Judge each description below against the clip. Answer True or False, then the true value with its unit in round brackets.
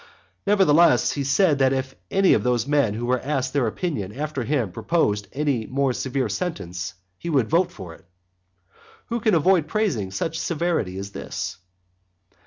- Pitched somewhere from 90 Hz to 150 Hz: True (140 Hz)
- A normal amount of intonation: False (6.9 semitones)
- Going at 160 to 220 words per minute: True (165 wpm)